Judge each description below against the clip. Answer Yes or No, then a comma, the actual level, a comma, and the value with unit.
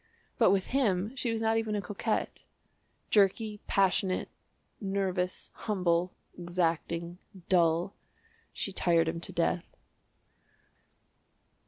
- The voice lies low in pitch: No, high, 190 Hz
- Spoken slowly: Yes, slow, 105 wpm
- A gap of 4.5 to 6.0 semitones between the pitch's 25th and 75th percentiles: No, average, 3.3 semitones